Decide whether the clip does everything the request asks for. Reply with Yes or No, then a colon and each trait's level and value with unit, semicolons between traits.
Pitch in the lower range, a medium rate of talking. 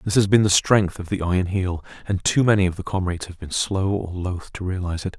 No: very low, 95 Hz; fast, 265 wpm